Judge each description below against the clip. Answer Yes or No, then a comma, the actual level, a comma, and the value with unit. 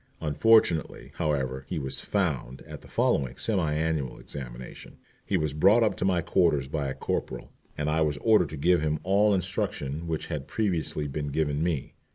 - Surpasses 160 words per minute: Yes, average, 180 wpm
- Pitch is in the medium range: No, very low, 75 Hz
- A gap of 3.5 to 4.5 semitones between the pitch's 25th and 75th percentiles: Yes, average, 3.9 semitones